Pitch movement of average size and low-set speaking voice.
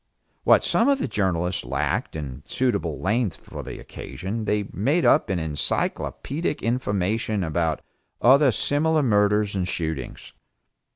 No: wide, 6.8 semitones; low, 100 Hz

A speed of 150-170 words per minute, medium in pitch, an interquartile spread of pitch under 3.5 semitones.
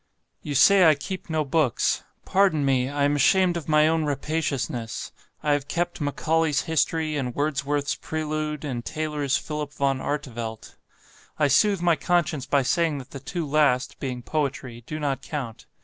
Yes: average, 165 wpm; medium, 150 Hz; narrow, 2.5 semitones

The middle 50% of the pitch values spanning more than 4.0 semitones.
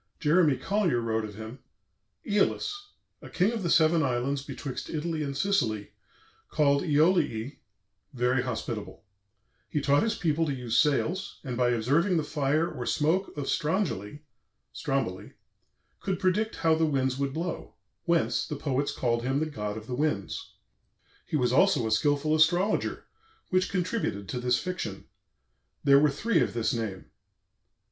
Yes: average, 5.3 semitones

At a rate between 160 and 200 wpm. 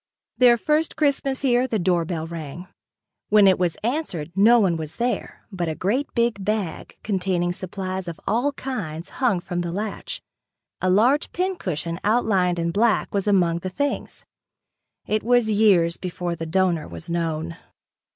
No: average, 150 wpm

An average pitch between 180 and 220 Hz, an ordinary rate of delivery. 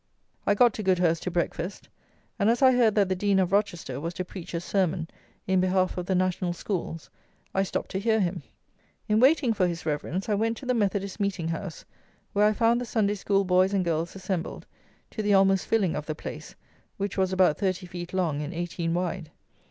No: high, 190 Hz; fast, 210 wpm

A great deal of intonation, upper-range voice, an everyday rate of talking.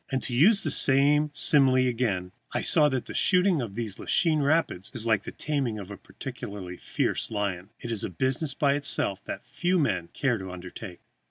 No: wide, 6.5 semitones; low, 125 Hz; average, 195 wpm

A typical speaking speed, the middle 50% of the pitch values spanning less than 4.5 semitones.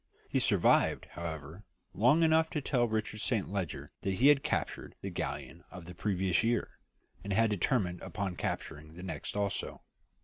No: average, 165 wpm; average, 5.1 semitones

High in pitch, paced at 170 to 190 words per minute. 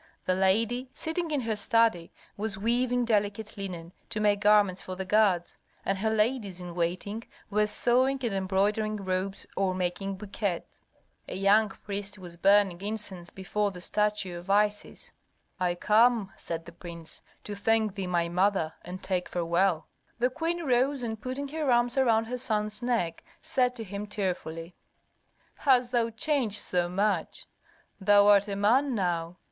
No: high, 205 Hz; average, 160 wpm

